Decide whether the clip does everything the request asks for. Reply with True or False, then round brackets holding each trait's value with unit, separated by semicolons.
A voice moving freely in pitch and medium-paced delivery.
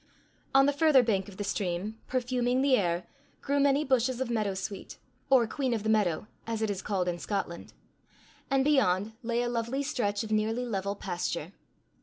False (4.6 semitones; 185 wpm)